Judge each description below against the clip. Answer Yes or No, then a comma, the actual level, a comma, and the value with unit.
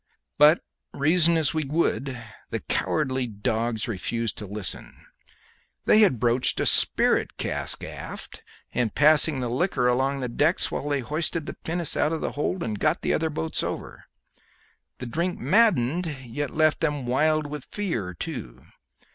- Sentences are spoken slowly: No, average, 155 wpm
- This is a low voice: No, medium, 145 Hz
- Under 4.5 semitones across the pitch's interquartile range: No, average, 4.9 semitones